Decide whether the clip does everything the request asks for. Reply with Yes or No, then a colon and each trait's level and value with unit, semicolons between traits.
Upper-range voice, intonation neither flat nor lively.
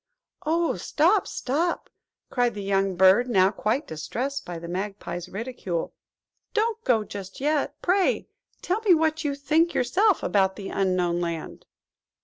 No: high, 240 Hz; wide, 8.8 semitones